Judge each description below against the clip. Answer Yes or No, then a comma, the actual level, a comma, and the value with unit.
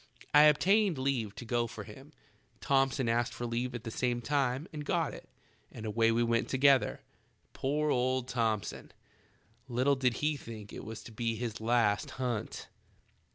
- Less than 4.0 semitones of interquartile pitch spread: Yes, average, 2.9 semitones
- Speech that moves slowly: No, average, 165 wpm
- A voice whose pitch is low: Yes, low, 120 Hz